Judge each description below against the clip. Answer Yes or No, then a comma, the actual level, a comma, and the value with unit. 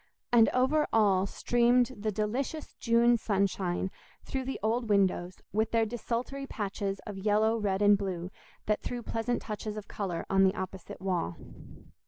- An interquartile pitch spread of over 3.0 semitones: Yes, average, 3.5 semitones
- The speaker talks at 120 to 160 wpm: Yes, average, 155 wpm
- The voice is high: Yes, high, 210 Hz